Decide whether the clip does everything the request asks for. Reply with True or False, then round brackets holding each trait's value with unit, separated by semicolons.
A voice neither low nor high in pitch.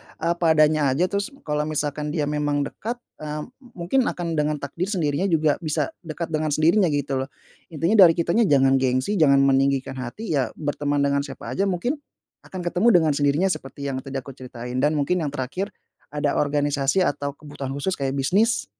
True (150 Hz)